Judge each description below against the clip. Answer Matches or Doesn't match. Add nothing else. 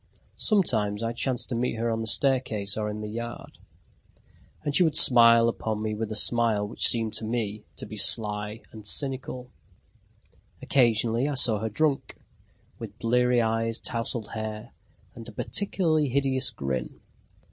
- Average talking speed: Matches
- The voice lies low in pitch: Matches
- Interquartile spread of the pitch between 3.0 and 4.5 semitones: Doesn't match